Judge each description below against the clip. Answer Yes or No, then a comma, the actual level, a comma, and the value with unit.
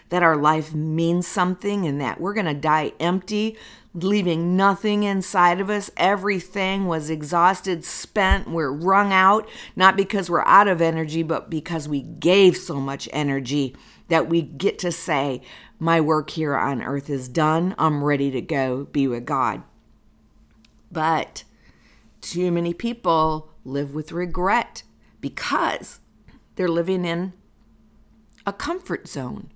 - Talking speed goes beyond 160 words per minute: No, average, 140 wpm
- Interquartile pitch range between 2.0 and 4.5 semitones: Yes, average, 3.9 semitones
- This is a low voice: No, medium, 170 Hz